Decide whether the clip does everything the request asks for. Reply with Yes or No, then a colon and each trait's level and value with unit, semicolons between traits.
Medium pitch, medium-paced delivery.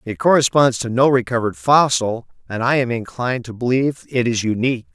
No: low, 125 Hz; average, 180 wpm